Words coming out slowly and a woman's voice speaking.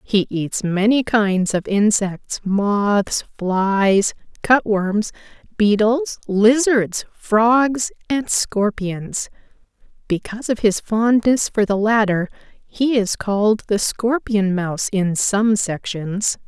Yes: slow, 110 wpm; female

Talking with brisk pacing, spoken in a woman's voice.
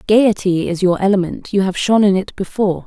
Yes: fast, 210 wpm; female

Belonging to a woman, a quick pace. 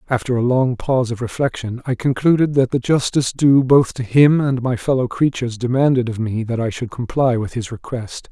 No: male; fast, 210 wpm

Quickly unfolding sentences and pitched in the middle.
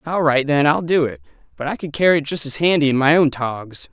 Yes: fast, 275 wpm; medium, 150 Hz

